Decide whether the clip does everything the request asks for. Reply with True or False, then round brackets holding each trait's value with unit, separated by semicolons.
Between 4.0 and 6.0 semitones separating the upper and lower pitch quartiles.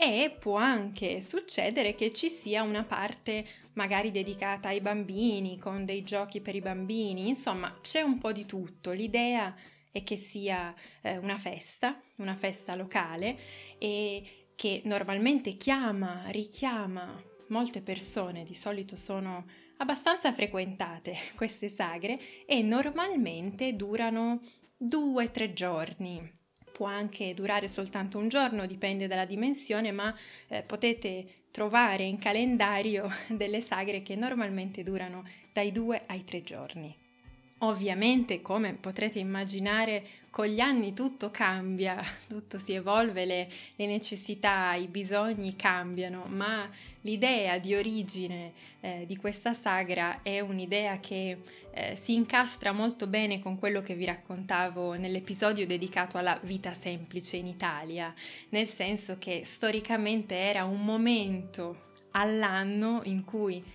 False (2.6 semitones)